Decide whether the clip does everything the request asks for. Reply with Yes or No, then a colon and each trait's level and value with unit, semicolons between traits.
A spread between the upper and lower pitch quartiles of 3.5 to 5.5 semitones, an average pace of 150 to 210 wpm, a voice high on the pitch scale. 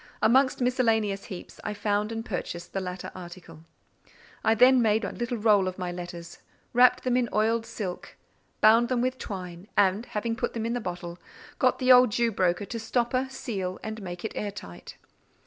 Yes: average, 4.4 semitones; average, 185 wpm; high, 215 Hz